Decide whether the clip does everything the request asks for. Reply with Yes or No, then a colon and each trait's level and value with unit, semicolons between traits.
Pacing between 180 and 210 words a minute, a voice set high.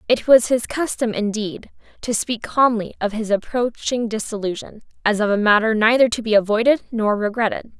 No: average, 170 wpm; high, 225 Hz